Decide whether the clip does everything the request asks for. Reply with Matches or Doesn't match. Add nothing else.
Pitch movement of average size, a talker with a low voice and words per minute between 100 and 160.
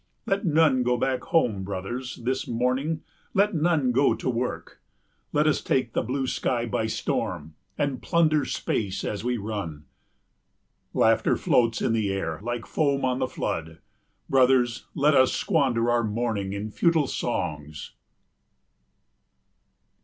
Matches